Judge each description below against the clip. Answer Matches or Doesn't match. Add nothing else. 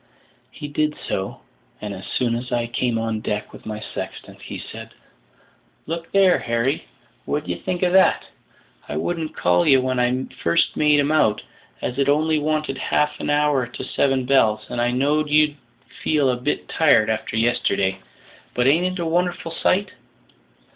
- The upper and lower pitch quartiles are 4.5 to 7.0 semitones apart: Matches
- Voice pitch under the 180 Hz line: Matches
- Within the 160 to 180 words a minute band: Matches